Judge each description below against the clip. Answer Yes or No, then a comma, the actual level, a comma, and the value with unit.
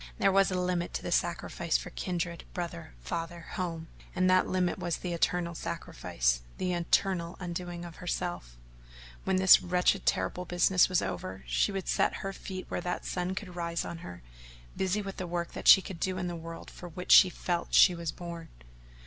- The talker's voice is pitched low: No, medium, 175 Hz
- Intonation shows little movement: Yes, narrow, 1.5 semitones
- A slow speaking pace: No, average, 190 wpm